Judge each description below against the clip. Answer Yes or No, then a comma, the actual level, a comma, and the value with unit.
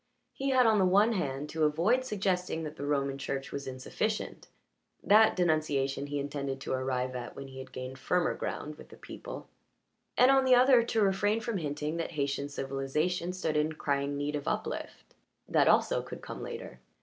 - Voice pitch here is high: No, medium, 150 Hz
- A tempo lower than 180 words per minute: No, average, 185 wpm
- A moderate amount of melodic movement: No, wide, 6.2 semitones